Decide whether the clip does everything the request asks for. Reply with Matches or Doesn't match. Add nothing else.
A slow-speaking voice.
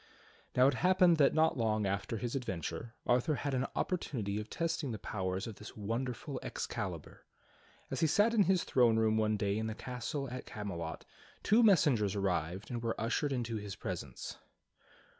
Doesn't match